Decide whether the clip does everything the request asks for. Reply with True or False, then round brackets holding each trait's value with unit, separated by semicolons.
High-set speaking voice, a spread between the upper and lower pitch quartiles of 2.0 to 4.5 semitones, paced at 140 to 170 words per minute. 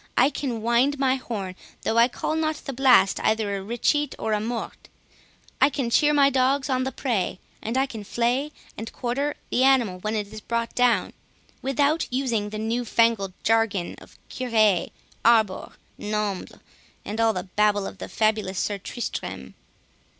True (230 Hz; 3.8 semitones; 165 wpm)